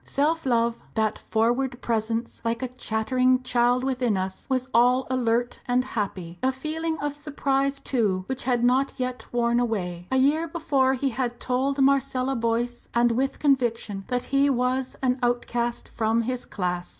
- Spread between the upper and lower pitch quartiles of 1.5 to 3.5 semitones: Yes, narrow, 2.4 semitones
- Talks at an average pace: Yes, average, 160 wpm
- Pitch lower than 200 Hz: No, very high, 250 Hz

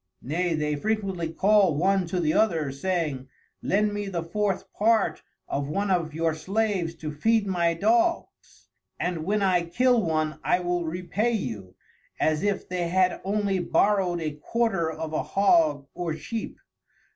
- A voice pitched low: No, medium, 180 Hz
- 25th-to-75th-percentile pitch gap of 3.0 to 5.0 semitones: Yes, average, 4.2 semitones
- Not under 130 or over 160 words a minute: Yes, average, 155 wpm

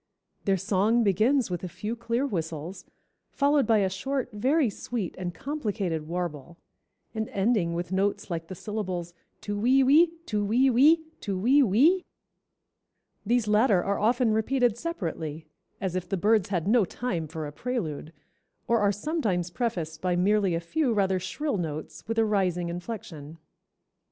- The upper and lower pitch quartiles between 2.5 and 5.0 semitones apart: No, wide, 5.4 semitones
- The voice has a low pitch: No, high, 205 Hz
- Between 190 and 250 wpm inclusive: No, average, 160 wpm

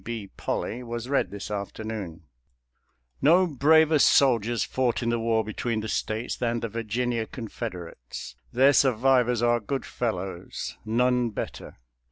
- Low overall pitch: Yes, low, 115 Hz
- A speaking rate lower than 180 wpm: Yes, average, 140 wpm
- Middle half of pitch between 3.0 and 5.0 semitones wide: No, narrow, 2.6 semitones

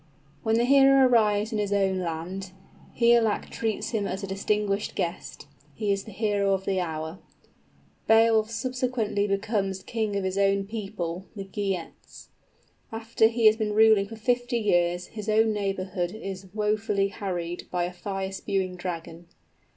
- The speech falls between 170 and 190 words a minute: No, average, 160 wpm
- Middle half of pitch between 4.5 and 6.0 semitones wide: No, average, 2.7 semitones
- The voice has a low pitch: No, high, 200 Hz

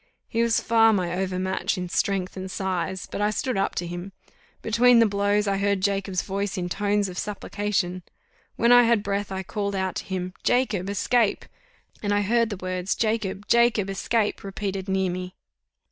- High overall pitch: Yes, high, 200 Hz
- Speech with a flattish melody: Yes, narrow, 2.2 semitones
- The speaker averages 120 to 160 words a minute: No, average, 180 wpm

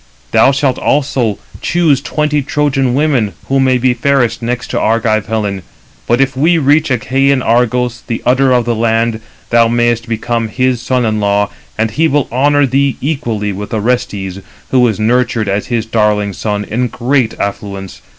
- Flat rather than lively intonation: No, average, 3.5 semitones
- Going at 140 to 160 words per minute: No, average, 170 wpm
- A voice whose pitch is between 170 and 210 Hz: No, low, 120 Hz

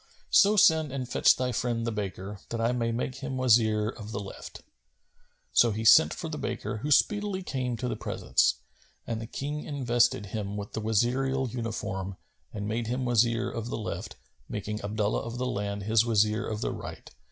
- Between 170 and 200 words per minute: Yes, average, 195 wpm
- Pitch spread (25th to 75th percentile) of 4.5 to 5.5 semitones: No, average, 3.1 semitones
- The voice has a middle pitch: No, low, 115 Hz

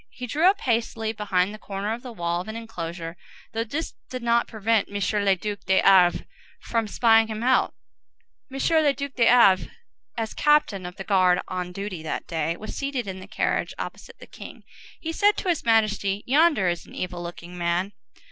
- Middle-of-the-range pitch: No, high, 210 Hz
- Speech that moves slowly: No, average, 195 wpm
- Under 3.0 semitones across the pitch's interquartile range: No, average, 4.4 semitones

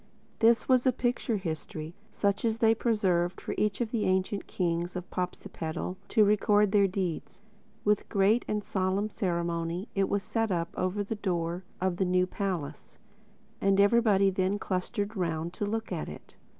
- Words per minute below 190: Yes, average, 165 wpm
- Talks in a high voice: Yes, high, 195 Hz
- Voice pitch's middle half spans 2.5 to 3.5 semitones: Yes, average, 2.8 semitones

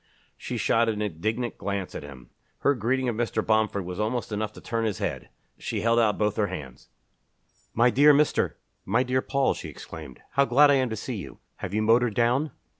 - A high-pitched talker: No, low, 115 Hz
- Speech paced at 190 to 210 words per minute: Yes, fast, 205 wpm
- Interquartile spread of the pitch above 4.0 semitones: No, average, 3.3 semitones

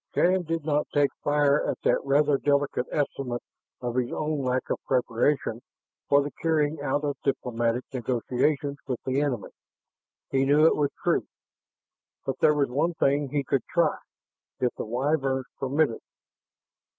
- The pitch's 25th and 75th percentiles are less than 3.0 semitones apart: Yes, narrow, 2.5 semitones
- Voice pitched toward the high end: No, medium, 140 Hz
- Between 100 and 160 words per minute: Yes, average, 150 wpm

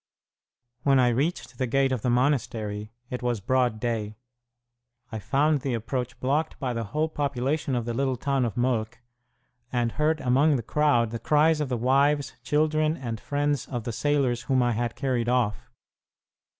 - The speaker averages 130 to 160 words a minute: No, average, 175 wpm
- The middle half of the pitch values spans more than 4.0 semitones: No, average, 3.4 semitones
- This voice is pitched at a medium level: No, low, 125 Hz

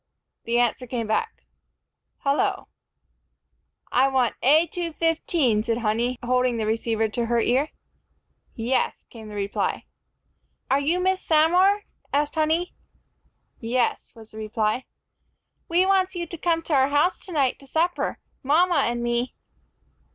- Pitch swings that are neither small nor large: No, wide, 5.9 semitones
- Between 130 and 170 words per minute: Yes, slow, 135 wpm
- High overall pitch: Yes, very high, 265 Hz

